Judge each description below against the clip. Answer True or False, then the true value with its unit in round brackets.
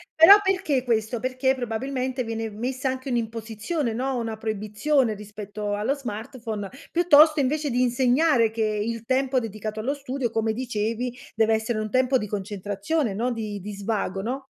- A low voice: False (235 Hz)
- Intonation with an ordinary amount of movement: True (3.4 semitones)